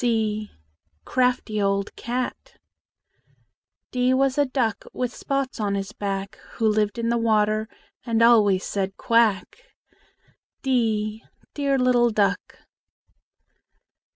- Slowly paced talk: Yes, slow, 110 wpm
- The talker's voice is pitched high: Yes, high, 225 Hz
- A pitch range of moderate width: Yes, average, 3.1 semitones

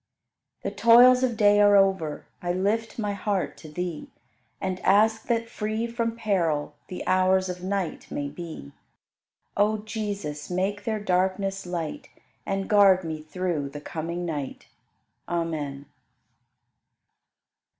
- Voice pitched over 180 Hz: Yes, high, 190 Hz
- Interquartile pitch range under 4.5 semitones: Yes, average, 3.8 semitones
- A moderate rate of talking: No, slow, 130 wpm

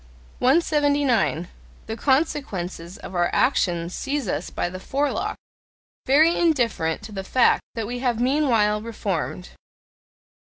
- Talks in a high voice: Yes, high, 230 Hz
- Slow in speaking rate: Yes, slow, 120 wpm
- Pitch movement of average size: No, wide, 6.9 semitones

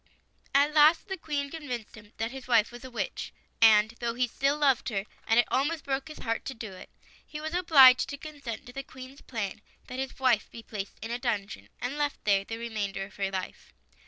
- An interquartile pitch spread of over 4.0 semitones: Yes, average, 4.4 semitones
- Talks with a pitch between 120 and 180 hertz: No, high, 245 Hz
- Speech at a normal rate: No, fast, 220 wpm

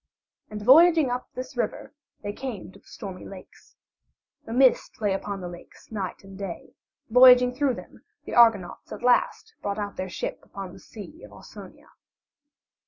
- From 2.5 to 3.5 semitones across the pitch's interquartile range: No, average, 4.5 semitones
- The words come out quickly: No, average, 170 wpm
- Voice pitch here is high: Yes, high, 220 Hz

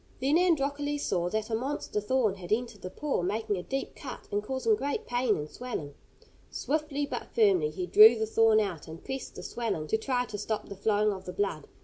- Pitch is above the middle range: Yes, high, 220 Hz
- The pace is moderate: No, fast, 215 wpm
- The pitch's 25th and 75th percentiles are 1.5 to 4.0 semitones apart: No, average, 5.1 semitones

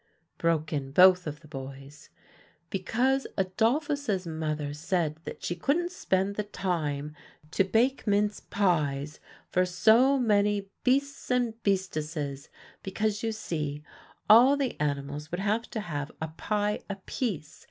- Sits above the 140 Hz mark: Yes, medium, 185 Hz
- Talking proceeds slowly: Yes, slow, 130 wpm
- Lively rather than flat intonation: Yes, wide, 6.3 semitones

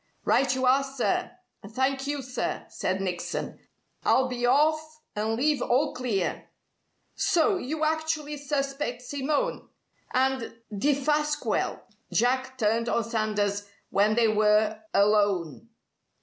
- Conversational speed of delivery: No, slow, 120 wpm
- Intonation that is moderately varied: Yes, average, 5.0 semitones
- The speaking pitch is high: Yes, very high, 255 Hz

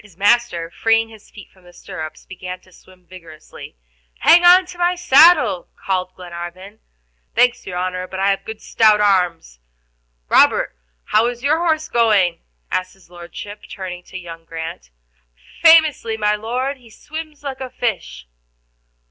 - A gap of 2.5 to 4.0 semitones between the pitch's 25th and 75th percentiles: No, wide, 5.5 semitones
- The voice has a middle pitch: No, high, 205 Hz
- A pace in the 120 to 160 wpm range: Yes, average, 155 wpm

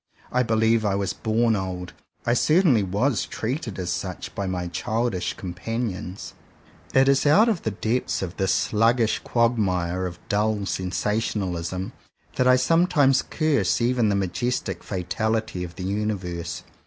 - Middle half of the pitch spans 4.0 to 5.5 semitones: Yes, average, 4.6 semitones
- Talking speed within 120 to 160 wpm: Yes, average, 140 wpm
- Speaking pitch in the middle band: No, low, 105 Hz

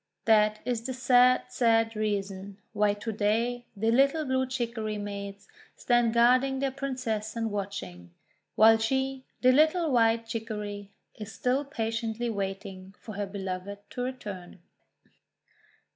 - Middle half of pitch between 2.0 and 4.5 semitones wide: Yes, average, 3.5 semitones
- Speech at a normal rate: No, slow, 130 wpm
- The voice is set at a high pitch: Yes, high, 225 Hz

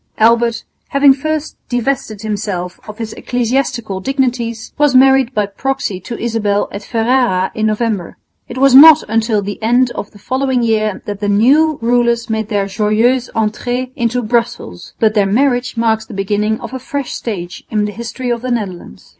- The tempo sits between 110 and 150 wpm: No, average, 170 wpm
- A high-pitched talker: Yes, high, 230 Hz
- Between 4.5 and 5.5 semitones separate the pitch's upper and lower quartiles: No, average, 3.3 semitones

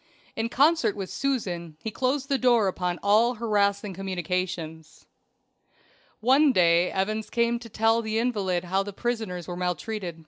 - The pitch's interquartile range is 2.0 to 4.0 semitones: No, average, 4.5 semitones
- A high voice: Yes, high, 205 Hz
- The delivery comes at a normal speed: Yes, average, 145 wpm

